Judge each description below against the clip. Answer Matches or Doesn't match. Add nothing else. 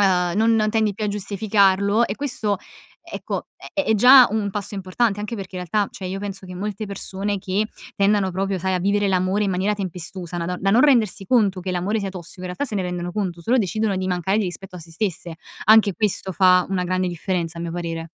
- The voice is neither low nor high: Doesn't match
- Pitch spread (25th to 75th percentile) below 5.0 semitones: Matches